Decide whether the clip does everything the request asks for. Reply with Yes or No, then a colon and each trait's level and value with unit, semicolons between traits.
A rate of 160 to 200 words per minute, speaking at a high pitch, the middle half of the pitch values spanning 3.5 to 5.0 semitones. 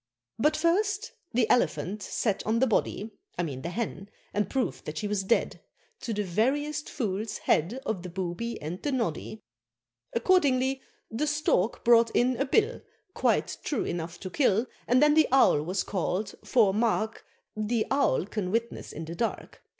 No: average, 170 wpm; high, 225 Hz; wide, 5.6 semitones